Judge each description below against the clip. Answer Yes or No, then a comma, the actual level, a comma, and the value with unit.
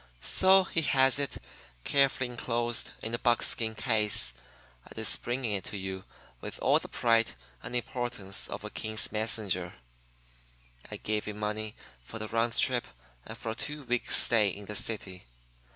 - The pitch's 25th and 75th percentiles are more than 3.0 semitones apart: No, narrow, 2.6 semitones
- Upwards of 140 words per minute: Yes, average, 170 wpm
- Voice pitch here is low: Yes, low, 115 Hz